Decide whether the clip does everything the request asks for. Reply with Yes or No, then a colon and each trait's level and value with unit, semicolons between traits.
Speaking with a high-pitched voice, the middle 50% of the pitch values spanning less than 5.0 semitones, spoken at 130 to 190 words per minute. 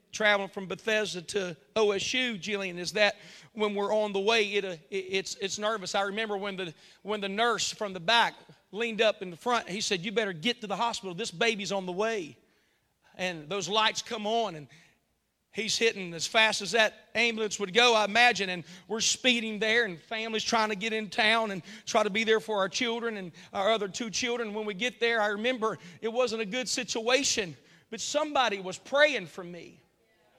No: high, 215 Hz; average, 2.7 semitones; fast, 205 wpm